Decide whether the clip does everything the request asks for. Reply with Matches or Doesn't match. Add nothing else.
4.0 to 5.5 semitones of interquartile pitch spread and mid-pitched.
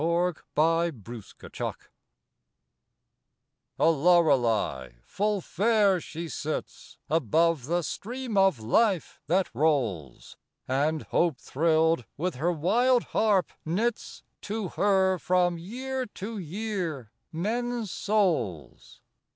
Matches